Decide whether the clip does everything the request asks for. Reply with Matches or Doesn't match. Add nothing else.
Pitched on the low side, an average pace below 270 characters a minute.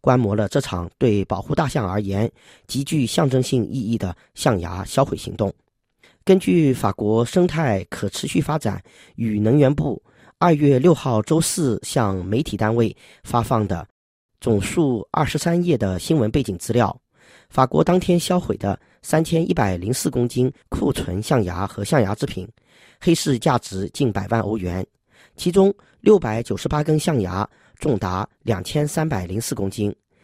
Matches